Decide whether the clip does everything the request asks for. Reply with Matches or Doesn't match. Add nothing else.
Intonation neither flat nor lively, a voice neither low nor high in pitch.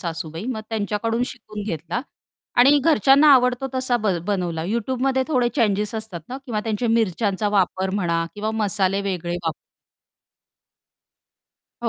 Doesn't match